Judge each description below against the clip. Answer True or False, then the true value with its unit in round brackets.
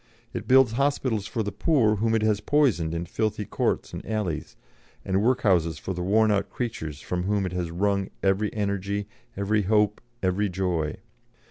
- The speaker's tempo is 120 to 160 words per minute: False (170 wpm)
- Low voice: True (100 Hz)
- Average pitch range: True (3.0 semitones)